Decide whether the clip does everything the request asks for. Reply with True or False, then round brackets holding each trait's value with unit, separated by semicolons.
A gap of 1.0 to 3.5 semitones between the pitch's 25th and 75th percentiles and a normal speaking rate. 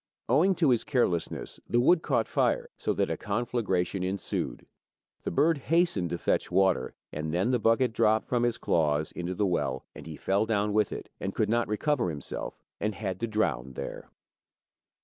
False (5.2 semitones; 185 wpm)